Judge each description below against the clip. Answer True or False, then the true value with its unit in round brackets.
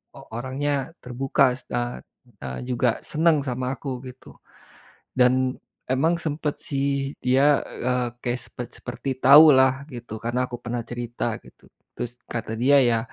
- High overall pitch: False (130 Hz)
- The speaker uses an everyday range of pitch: False (2.3 semitones)